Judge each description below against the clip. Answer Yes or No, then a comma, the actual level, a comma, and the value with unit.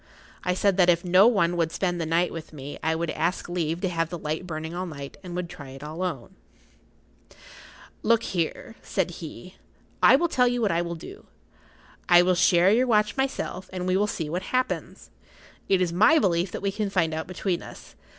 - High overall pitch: No, medium, 180 Hz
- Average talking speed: No, fast, 210 wpm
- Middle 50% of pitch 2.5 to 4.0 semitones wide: Yes, average, 3.0 semitones